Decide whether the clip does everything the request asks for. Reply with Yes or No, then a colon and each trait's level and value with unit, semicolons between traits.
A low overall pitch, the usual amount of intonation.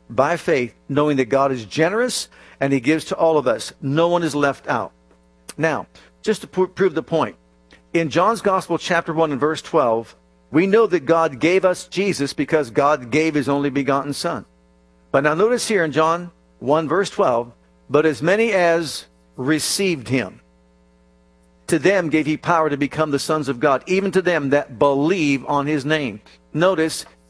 No: medium, 150 Hz; average, 5.0 semitones